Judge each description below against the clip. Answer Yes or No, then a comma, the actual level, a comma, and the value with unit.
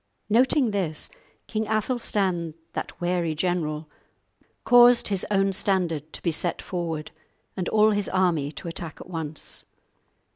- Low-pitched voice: No, medium, 180 Hz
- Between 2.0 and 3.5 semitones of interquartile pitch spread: No, average, 4.3 semitones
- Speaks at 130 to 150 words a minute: Yes, slow, 135 wpm